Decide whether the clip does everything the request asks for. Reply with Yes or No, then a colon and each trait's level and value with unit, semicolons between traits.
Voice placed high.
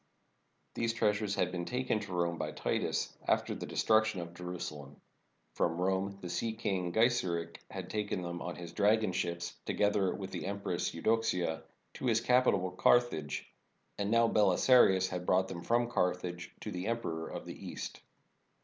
No: very low, 95 Hz